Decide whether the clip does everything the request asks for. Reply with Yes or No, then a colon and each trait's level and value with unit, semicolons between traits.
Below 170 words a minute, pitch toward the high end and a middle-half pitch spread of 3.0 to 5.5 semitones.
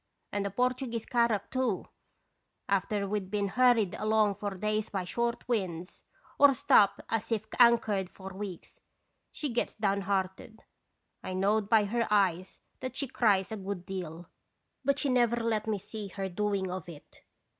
Yes: average, 160 wpm; high, 210 Hz; average, 3.3 semitones